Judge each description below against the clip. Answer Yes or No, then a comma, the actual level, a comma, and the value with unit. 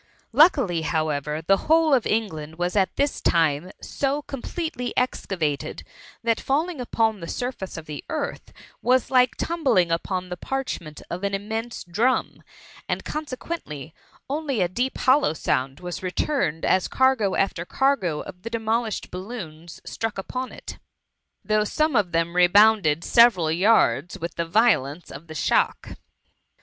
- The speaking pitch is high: Yes, high, 200 Hz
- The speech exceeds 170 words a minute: No, average, 145 wpm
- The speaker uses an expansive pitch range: Yes, wide, 7.2 semitones